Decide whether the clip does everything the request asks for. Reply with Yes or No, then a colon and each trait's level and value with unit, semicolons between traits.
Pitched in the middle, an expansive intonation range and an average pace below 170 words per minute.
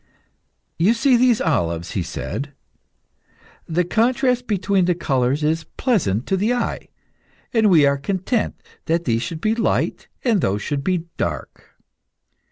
Yes: medium, 175 Hz; wide, 8.0 semitones; average, 145 wpm